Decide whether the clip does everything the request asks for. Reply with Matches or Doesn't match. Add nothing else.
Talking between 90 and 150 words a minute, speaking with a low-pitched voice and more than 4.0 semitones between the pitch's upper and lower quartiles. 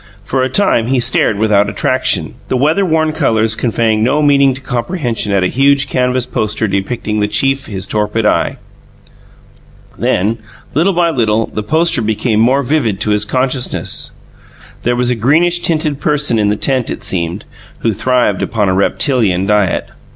Doesn't match